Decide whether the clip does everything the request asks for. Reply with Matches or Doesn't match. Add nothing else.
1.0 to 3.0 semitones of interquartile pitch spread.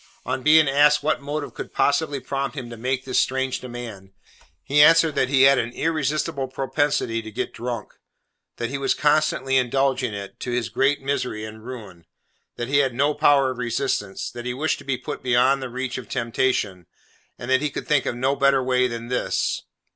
Matches